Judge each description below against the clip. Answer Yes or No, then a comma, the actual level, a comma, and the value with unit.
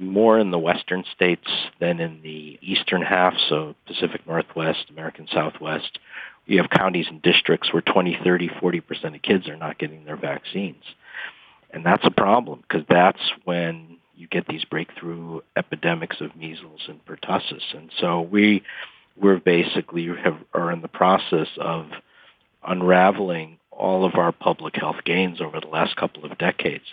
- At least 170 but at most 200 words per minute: No, average, 160 wpm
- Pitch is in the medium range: No, very low, 85 Hz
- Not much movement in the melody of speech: Yes, narrow, 2.0 semitones